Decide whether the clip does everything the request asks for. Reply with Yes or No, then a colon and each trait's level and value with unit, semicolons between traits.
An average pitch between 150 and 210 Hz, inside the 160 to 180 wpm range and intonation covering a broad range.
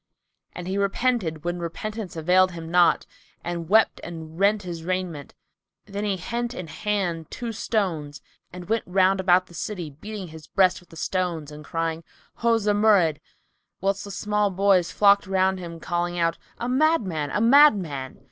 No: medium, 185 Hz; average, 165 wpm; average, 3.7 semitones